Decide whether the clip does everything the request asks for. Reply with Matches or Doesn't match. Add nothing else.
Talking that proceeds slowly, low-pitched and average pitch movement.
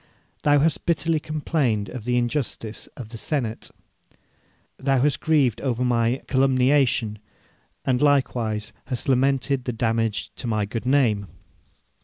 Matches